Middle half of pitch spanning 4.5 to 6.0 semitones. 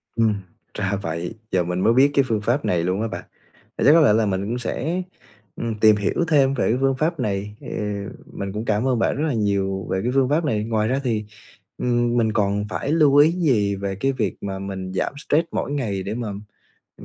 Yes: average, 5.2 semitones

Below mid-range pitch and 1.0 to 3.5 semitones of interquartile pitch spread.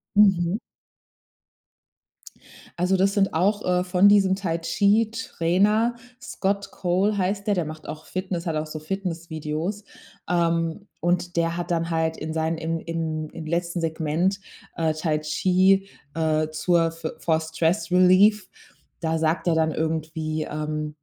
No: medium, 170 Hz; average, 3.1 semitones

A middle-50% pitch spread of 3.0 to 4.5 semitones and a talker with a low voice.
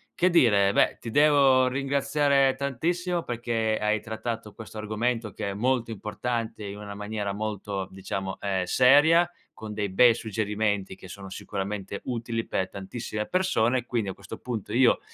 Yes: average, 4.0 semitones; low, 110 Hz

